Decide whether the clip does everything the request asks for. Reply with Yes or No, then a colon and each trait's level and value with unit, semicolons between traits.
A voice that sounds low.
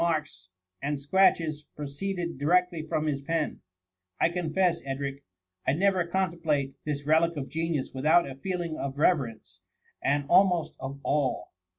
No: medium, 155 Hz